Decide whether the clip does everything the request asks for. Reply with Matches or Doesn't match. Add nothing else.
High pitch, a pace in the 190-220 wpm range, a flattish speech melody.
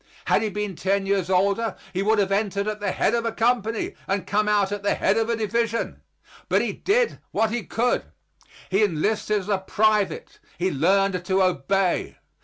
Matches